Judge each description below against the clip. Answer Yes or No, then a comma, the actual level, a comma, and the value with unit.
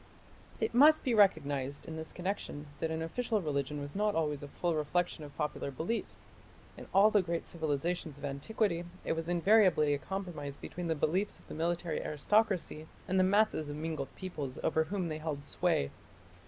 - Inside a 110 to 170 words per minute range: No, average, 180 wpm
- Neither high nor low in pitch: Yes, medium, 165 Hz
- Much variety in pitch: No, average, 4.2 semitones